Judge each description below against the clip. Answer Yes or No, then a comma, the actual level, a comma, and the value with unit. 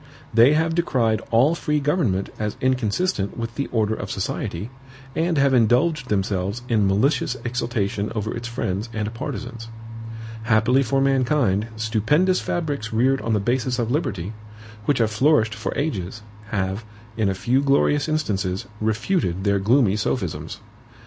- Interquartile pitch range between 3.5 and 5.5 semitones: Yes, average, 4.6 semitones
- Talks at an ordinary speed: Yes, average, 145 wpm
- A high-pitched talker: No, low, 115 Hz